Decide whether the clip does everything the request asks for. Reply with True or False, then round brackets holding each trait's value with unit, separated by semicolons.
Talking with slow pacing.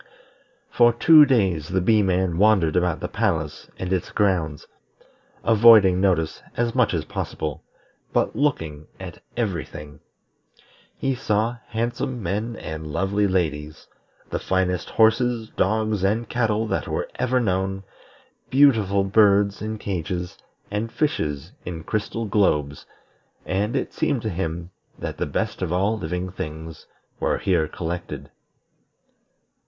True (130 wpm)